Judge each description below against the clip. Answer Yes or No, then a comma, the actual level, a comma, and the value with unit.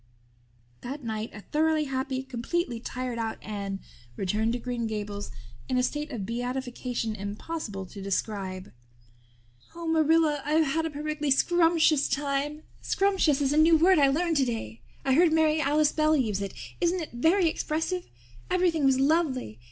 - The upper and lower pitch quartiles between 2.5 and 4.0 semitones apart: No, wide, 5.6 semitones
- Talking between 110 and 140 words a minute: No, average, 155 wpm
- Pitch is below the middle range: No, very high, 275 Hz